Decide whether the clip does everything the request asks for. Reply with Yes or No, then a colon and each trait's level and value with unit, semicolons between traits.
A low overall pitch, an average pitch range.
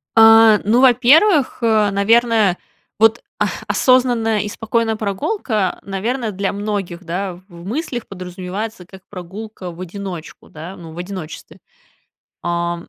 No: high, 205 Hz; average, 3.8 semitones